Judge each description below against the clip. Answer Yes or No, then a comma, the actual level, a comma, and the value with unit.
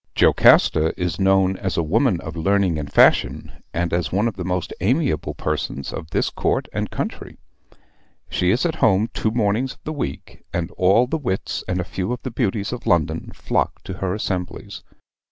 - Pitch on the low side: Yes, very low, 95 Hz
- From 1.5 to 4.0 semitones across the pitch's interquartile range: No, average, 4.6 semitones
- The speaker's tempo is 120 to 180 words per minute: No, average, 190 wpm